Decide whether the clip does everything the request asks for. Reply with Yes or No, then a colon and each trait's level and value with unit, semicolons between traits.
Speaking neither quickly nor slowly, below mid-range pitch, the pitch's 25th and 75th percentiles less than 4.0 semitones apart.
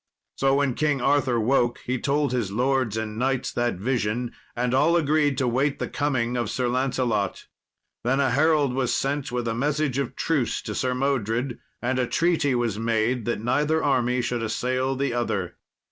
Yes: average, 180 wpm; low, 125 Hz; narrow, 2.6 semitones